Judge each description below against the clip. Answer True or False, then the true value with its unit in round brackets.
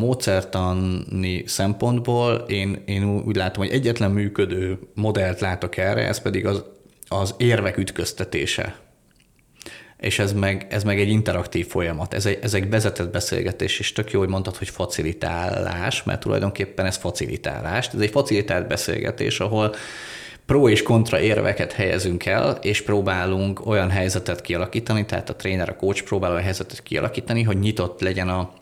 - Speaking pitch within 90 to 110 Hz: True (100 Hz)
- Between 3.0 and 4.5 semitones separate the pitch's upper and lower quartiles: False (2.5 semitones)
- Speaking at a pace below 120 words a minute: False (145 wpm)